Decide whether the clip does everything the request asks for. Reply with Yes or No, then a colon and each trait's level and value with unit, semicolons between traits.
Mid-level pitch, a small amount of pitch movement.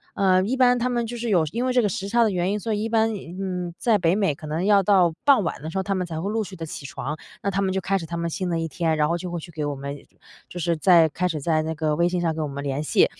No: medium, 180 Hz; average, 4.2 semitones